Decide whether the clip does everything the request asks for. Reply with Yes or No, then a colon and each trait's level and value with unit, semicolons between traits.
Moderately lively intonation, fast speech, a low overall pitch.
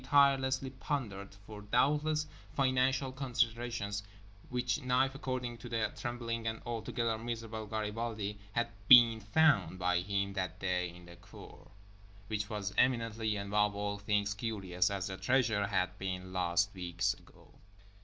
No: average, 3.8 semitones; slow, 135 wpm; low, 110 Hz